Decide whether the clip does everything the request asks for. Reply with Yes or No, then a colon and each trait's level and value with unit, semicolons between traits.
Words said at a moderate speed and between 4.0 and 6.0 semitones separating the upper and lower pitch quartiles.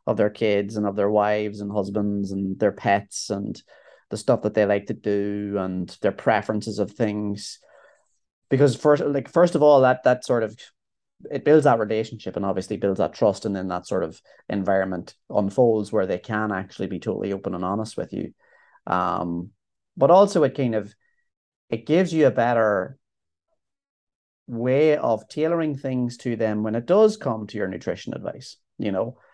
Yes: average, 180 wpm; average, 4.4 semitones